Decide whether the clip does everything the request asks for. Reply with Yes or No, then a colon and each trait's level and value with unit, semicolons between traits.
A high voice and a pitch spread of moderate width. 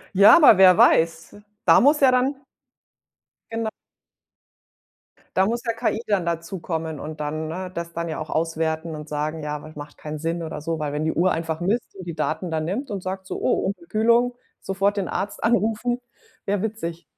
No: medium, 175 Hz; average, 5.0 semitones